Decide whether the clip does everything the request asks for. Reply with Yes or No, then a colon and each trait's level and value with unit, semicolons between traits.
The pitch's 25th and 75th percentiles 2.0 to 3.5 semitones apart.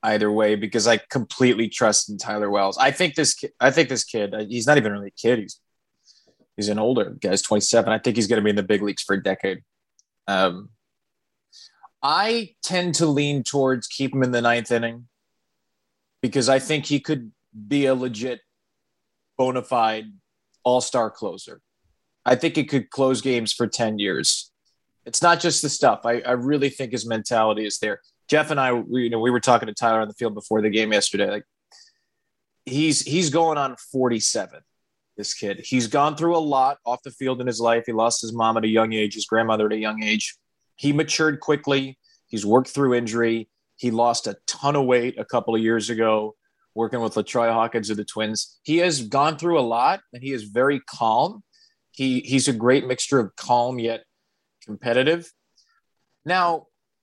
No: average, 4.0 semitones